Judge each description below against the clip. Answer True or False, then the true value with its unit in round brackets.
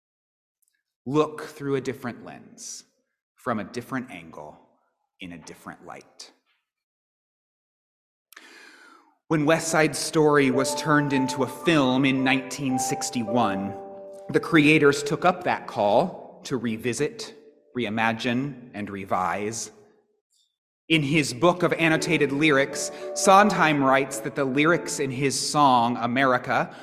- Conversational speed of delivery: False (110 wpm)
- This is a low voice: False (145 Hz)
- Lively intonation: False (4.9 semitones)